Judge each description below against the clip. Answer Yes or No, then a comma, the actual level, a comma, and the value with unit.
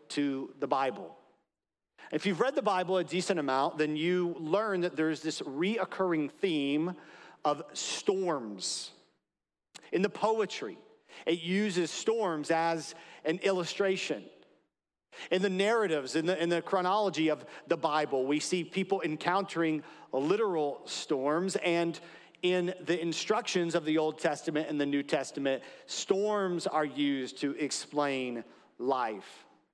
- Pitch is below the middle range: No, medium, 170 Hz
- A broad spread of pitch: No, average, 3.7 semitones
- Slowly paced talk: Yes, slow, 130 wpm